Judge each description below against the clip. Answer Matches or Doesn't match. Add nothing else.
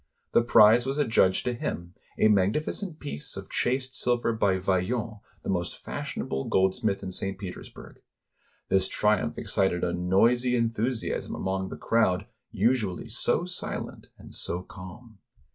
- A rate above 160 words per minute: Doesn't match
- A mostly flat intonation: Doesn't match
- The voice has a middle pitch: Doesn't match